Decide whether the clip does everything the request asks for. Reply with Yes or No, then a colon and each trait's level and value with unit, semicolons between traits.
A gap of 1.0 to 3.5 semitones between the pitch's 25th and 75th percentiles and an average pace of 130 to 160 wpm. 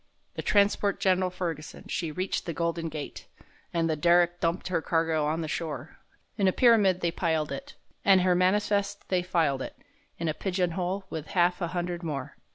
No: narrow, 2.4 semitones; average, 180 wpm